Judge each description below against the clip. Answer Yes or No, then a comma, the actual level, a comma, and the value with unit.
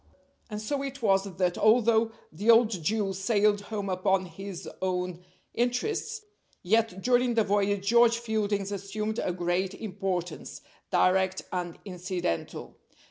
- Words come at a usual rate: No, slow, 130 wpm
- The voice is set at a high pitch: Yes, high, 200 Hz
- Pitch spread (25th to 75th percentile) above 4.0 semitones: No, average, 3.3 semitones